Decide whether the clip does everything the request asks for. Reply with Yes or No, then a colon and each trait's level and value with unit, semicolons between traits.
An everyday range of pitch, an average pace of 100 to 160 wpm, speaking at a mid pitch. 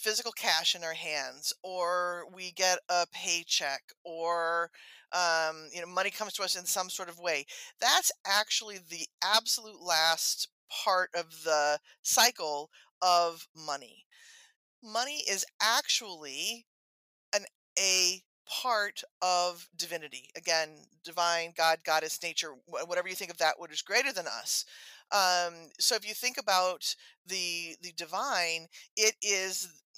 Yes: average, 3.3 semitones; slow, 135 wpm; medium, 180 Hz